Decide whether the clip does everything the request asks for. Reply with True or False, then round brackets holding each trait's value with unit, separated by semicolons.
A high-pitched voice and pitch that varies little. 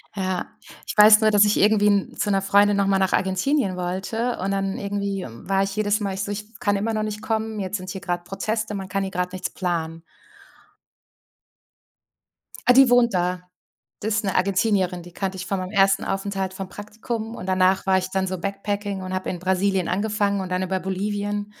True (195 Hz; 1.8 semitones)